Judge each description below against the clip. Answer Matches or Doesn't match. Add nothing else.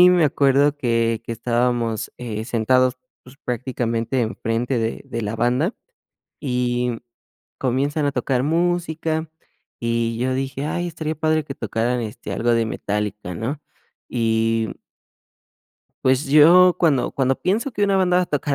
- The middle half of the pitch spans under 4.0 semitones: Doesn't match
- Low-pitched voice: Matches